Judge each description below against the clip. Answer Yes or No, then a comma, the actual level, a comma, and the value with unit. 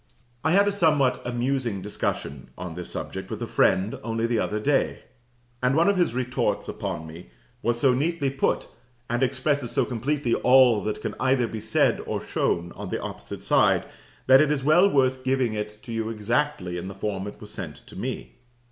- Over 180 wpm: Yes, average, 195 wpm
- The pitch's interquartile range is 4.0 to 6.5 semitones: Yes, average, 4.5 semitones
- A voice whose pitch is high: No, low, 120 Hz